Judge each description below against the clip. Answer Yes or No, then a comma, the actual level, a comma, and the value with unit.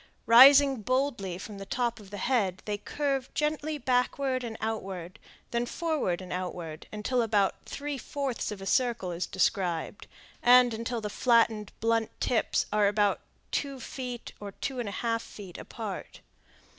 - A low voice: No, high, 230 Hz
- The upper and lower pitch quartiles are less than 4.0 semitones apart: No, average, 4.3 semitones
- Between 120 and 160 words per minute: Yes, average, 155 wpm